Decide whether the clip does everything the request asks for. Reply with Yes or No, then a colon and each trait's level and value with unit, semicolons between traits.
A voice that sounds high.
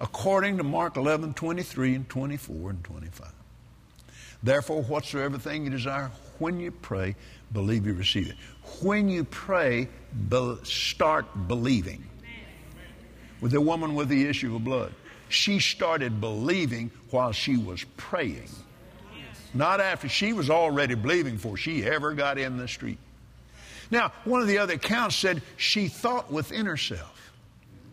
No: low, 135 Hz